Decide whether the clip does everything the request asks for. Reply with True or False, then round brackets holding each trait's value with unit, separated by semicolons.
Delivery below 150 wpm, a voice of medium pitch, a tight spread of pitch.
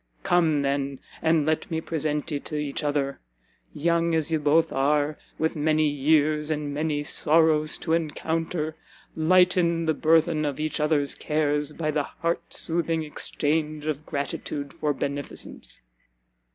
True (140 wpm; 155 Hz; 1.6 semitones)